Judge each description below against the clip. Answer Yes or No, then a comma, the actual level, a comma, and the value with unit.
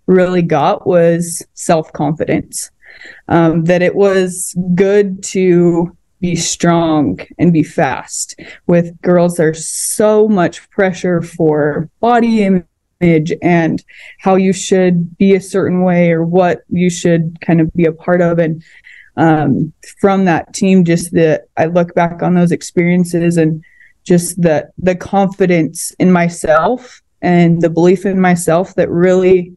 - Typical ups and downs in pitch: No, narrow, 1.9 semitones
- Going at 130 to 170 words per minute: Yes, average, 140 wpm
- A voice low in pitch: No, medium, 175 Hz